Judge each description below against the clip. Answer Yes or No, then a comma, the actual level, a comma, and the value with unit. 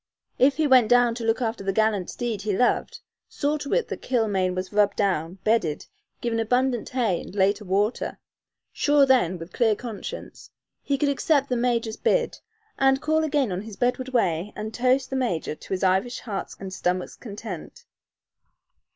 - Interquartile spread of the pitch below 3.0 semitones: No, average, 4.7 semitones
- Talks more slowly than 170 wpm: No, average, 175 wpm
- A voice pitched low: No, high, 225 Hz